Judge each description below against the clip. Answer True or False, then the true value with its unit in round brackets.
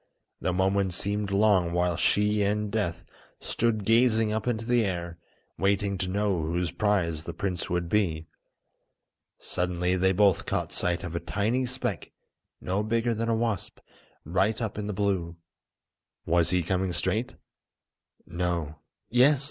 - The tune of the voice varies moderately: True (3.4 semitones)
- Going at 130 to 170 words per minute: True (150 wpm)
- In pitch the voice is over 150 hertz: False (100 Hz)